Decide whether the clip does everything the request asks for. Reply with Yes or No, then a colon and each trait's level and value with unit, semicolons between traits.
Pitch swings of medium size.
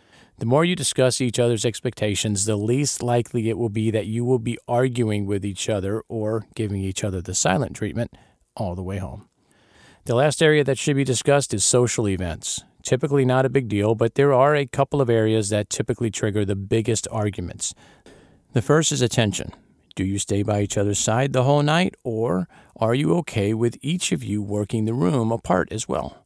Yes: average, 3.7 semitones